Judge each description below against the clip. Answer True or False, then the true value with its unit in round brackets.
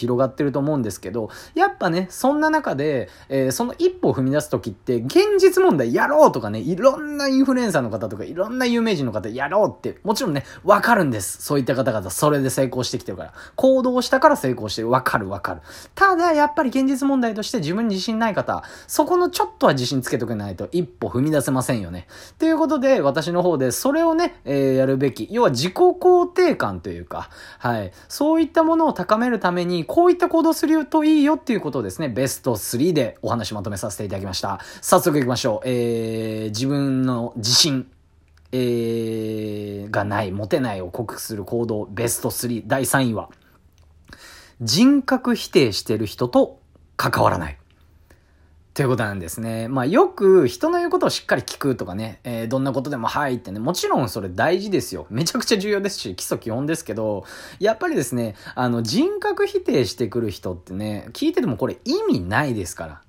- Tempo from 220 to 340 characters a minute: False (400 characters per minute)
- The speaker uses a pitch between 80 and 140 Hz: True (135 Hz)